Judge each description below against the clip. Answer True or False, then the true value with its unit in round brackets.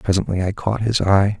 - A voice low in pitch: True (100 Hz)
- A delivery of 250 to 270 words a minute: False (215 wpm)